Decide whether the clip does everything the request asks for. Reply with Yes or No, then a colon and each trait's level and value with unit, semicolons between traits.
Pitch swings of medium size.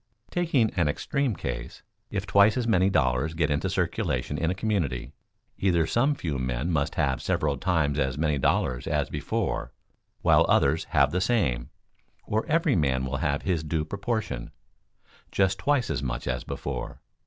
No: wide, 6.7 semitones